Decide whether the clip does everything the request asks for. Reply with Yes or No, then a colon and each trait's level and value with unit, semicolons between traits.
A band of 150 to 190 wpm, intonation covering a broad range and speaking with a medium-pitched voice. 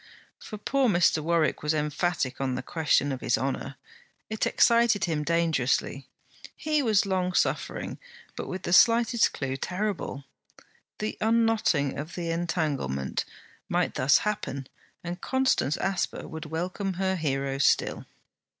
No: slow, 135 wpm; wide, 6.3 semitones; medium, 170 Hz